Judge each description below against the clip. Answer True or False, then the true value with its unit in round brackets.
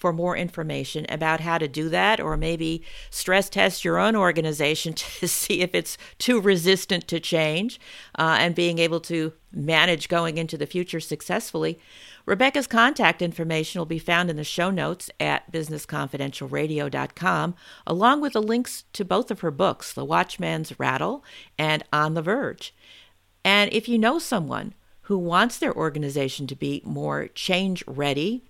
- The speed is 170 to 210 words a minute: False (160 wpm)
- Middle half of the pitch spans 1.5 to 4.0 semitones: True (3.6 semitones)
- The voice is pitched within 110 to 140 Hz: False (170 Hz)